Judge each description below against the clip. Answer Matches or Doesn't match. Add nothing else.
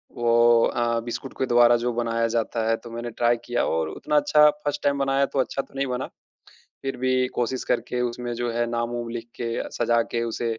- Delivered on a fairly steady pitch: Matches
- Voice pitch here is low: Matches